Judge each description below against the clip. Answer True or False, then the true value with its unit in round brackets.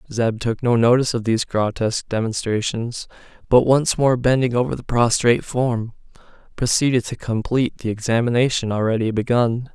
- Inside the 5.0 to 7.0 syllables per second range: True (5.5 syllables/s)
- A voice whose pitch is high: False (120 Hz)